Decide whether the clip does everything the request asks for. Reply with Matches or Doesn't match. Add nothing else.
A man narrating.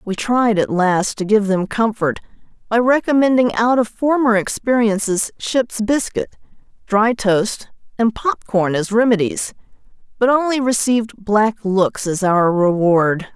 Doesn't match